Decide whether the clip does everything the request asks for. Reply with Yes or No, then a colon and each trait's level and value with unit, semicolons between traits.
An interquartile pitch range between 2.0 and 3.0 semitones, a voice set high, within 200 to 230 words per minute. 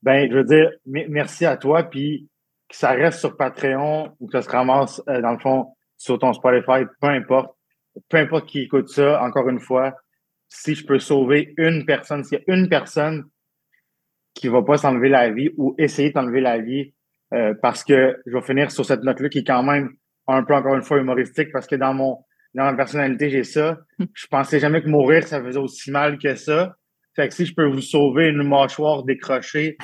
No: narrow, 2.4 semitones; medium, 140 Hz; average, 215 wpm